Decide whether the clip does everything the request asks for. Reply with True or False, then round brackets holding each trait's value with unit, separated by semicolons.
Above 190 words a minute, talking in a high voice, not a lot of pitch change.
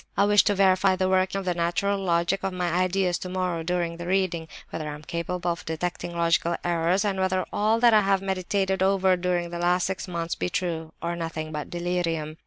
False (205 wpm; 180 Hz; 2.0 semitones)